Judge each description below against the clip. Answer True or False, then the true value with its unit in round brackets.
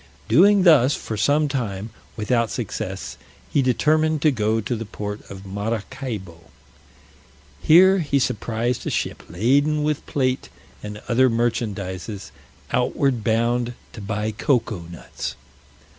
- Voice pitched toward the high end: False (115 Hz)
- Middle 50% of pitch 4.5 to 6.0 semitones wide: True (5.0 semitones)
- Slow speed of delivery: True (125 wpm)